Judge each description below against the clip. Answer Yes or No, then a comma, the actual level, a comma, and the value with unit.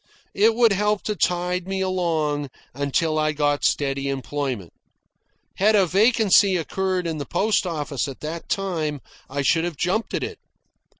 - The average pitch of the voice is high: No, medium, 170 Hz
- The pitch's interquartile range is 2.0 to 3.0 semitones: No, average, 4.8 semitones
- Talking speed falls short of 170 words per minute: Yes, average, 160 wpm